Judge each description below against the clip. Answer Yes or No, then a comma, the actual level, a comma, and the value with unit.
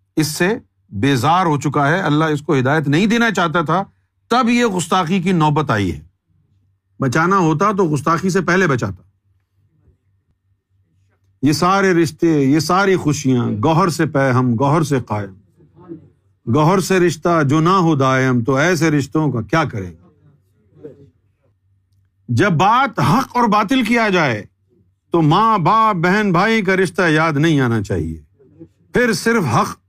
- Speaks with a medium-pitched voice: Yes, medium, 150 Hz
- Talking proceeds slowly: No, average, 155 wpm